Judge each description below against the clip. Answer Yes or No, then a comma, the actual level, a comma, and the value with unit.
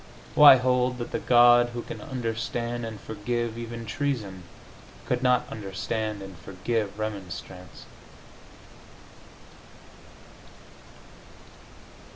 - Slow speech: Yes, slow, 90 wpm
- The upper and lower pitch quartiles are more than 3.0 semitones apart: No, average, 2.7 semitones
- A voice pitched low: Yes, low, 115 Hz